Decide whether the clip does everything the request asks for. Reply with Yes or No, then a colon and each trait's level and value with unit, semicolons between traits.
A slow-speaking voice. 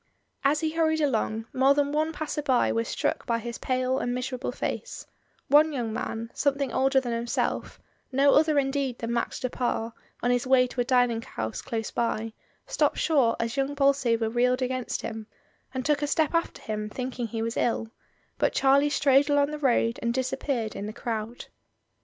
No: average, 190 wpm